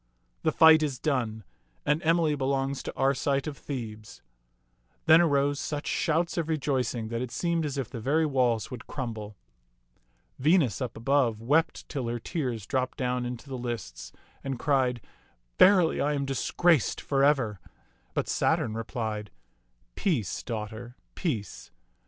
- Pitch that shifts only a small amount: No, average, 4.3 semitones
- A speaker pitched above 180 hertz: No, low, 135 Hz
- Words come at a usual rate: Yes, average, 145 wpm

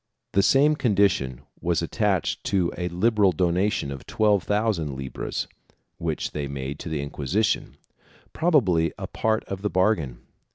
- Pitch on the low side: Yes, very low, 90 Hz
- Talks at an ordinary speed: Yes, average, 155 wpm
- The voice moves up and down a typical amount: No, wide, 5.8 semitones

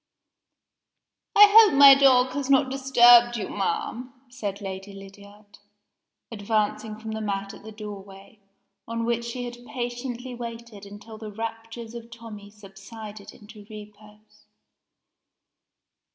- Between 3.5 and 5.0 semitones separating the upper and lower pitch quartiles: No, average, 2.8 semitones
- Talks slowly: Yes, slow, 125 wpm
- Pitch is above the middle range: Yes, high, 225 Hz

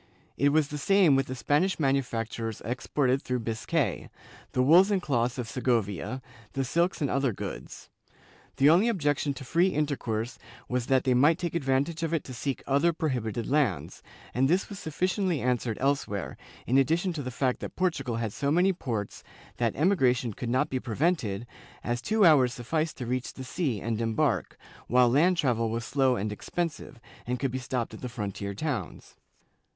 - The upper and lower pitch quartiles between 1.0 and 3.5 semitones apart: No, average, 4.6 semitones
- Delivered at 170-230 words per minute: Yes, average, 180 wpm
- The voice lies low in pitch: Yes, low, 130 Hz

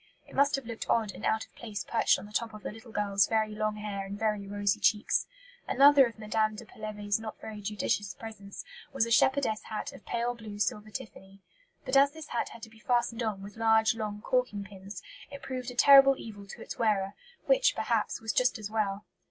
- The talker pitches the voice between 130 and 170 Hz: No, high, 220 Hz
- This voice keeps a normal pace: No, fast, 220 wpm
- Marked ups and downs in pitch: No, narrow, 2.6 semitones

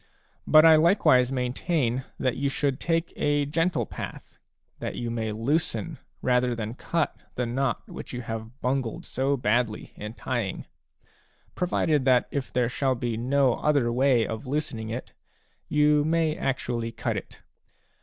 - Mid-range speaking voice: No, low, 130 Hz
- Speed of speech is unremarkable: Yes, average, 155 wpm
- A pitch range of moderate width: Yes, average, 3.8 semitones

